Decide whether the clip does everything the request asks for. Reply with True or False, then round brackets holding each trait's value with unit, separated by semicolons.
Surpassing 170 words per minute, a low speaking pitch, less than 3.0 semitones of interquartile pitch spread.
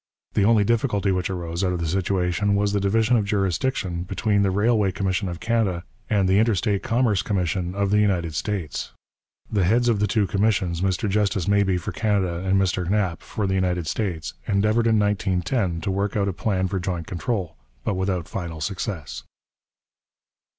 True (180 wpm; 95 Hz; 2.6 semitones)